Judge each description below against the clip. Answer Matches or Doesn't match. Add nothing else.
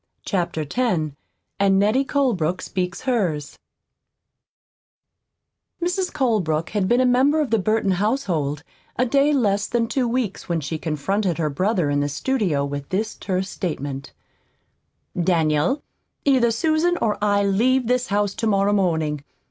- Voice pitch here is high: Matches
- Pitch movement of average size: Doesn't match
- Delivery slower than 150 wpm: Matches